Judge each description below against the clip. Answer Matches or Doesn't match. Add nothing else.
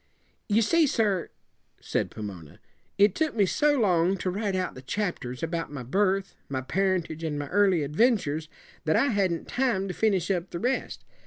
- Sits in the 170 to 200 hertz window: Matches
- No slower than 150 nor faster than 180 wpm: Matches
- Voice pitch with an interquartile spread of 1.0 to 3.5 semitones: Doesn't match